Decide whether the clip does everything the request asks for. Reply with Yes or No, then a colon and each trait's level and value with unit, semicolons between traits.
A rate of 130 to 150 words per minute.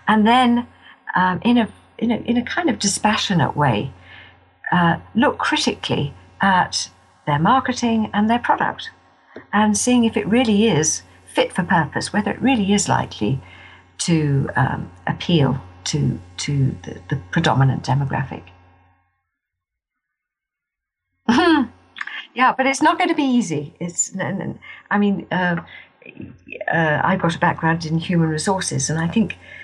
Yes: average, 140 wpm